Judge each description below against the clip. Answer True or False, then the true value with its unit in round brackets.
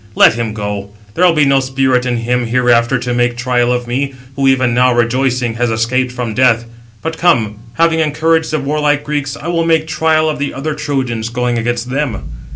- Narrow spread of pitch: False (3.5 semitones)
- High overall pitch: False (125 Hz)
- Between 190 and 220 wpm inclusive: True (200 wpm)